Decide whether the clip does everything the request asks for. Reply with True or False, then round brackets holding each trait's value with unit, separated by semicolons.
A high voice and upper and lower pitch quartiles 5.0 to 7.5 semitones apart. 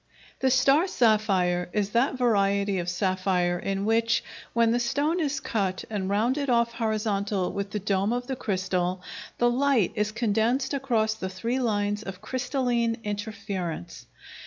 False (215 Hz; 3.6 semitones)